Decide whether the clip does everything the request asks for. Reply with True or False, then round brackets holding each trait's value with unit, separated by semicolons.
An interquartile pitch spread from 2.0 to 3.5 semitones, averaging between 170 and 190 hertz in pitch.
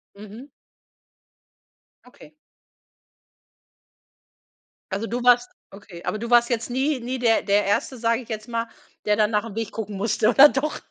False (2.7 semitones; 230 Hz)